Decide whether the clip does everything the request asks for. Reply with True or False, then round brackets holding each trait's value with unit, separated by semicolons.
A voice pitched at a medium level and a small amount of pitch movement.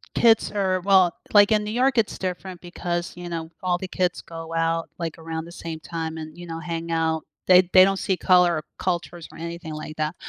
True (175 Hz; 2.1 semitones)